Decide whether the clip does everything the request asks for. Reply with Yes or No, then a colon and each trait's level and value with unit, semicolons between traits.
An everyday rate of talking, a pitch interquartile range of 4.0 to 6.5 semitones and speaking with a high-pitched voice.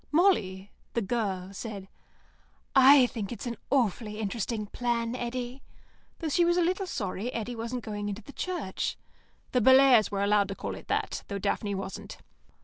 Yes: average, 165 wpm; average, 4.3 semitones; high, 230 Hz